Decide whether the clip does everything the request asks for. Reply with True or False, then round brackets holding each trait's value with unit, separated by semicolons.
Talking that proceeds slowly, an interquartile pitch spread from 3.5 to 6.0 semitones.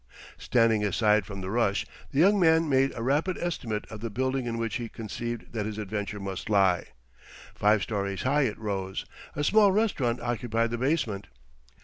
False (175 wpm; 4.3 semitones)